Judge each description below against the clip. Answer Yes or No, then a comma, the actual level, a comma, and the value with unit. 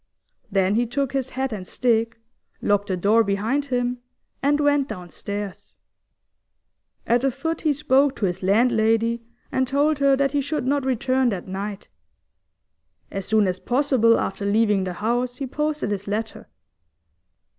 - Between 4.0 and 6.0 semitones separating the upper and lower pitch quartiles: Yes, average, 4.9 semitones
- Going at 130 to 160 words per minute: Yes, average, 155 wpm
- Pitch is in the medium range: No, high, 235 Hz